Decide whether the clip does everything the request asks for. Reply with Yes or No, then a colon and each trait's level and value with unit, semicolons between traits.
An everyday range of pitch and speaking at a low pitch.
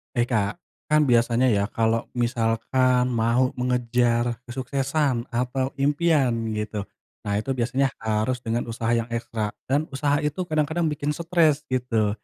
Yes: average, 3.2 semitones; low, 125 Hz